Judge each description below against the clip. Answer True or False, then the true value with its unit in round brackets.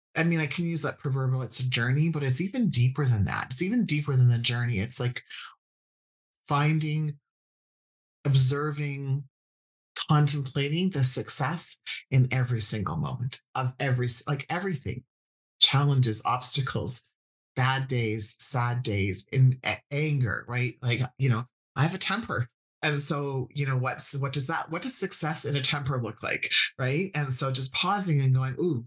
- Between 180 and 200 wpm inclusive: False (160 wpm)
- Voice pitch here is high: False (135 Hz)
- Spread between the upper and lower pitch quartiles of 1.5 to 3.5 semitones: True (3.2 semitones)